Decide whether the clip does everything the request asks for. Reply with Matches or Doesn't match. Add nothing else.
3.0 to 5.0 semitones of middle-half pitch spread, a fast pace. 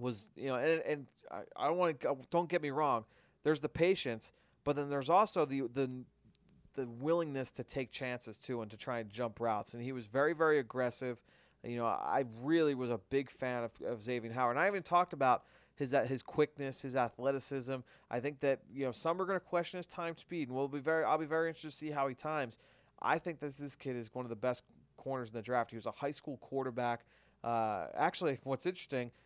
Matches